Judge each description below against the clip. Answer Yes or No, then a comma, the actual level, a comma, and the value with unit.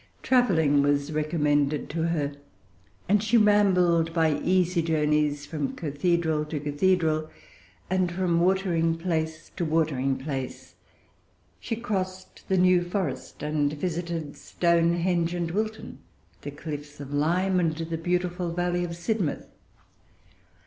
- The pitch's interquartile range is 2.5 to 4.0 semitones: Yes, average, 3.1 semitones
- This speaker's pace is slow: Yes, slow, 120 wpm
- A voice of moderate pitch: Yes, medium, 165 Hz